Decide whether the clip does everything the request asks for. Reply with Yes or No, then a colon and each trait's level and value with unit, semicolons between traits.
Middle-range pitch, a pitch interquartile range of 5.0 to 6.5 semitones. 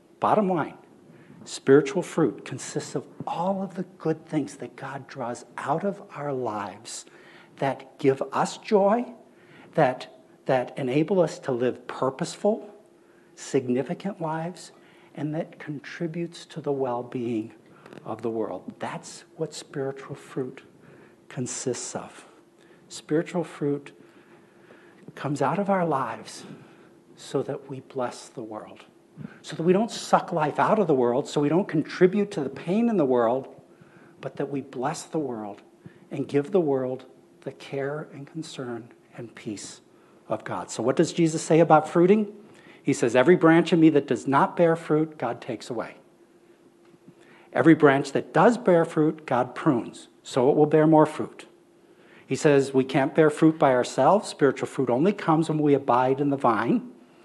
No: medium, 155 Hz; average, 4.2 semitones